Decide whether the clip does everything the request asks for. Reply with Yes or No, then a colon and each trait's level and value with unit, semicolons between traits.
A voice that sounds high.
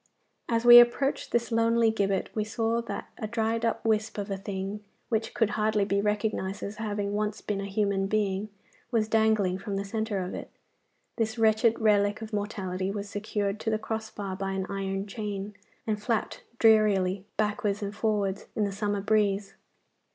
Yes: high, 210 Hz